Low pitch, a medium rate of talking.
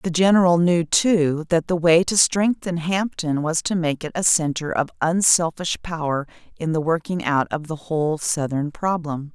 No: medium, 165 Hz; average, 180 wpm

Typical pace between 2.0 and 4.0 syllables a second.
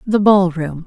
Yes: 3.9 syllables/s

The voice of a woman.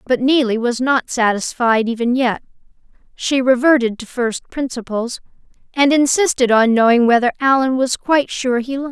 Yes: female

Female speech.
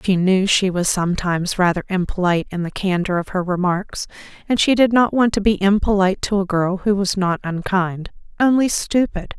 Yes: female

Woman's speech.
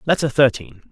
No: male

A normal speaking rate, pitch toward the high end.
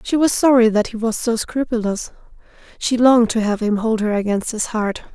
No: fast, 210 wpm; high, 225 Hz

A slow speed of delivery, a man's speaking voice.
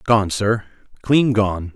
Yes: slow, 105 wpm; male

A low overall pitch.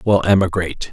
Yes: very low, 95 Hz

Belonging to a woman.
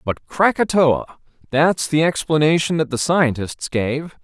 No: male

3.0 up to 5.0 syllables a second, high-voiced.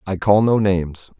No: 4.9 syllables/s; very low, 95 Hz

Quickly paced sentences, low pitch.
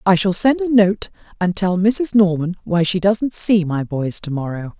No: fast, 215 wpm; high, 190 Hz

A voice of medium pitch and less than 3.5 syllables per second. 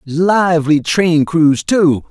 Yes: medium, 160 Hz; 3.1 syllables/s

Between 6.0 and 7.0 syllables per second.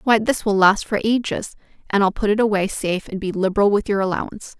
Yes: 6.4 syllables/s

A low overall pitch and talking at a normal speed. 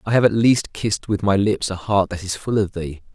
No: low, 100 Hz; fast, 285 wpm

